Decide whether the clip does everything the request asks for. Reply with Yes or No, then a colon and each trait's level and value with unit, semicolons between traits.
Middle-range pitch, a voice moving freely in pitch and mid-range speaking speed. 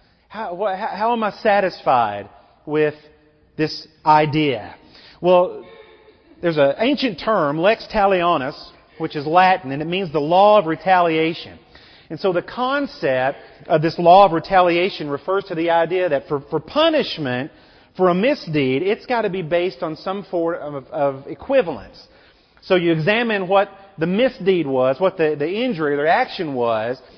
No: medium, 175 Hz; average, 4.7 semitones; average, 160 wpm